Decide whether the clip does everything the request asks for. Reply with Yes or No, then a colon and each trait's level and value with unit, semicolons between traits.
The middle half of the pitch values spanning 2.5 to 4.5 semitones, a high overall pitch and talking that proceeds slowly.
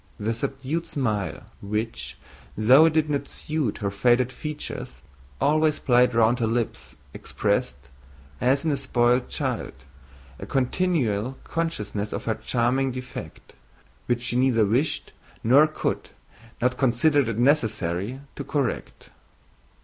No: average, 4.2 semitones; low, 125 Hz; slow, 125 wpm